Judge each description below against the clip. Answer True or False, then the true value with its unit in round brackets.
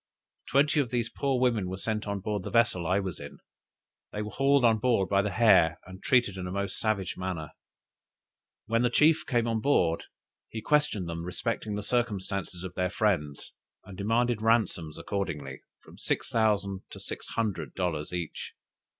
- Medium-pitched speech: False (105 Hz)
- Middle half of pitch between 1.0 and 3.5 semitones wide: False (4.1 semitones)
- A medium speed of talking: True (175 wpm)